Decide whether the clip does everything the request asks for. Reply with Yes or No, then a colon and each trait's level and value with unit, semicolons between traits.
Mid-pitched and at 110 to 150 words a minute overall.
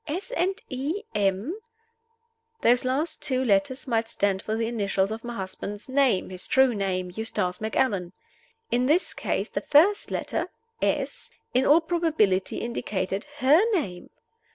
No: high, 235 Hz; average, 145 wpm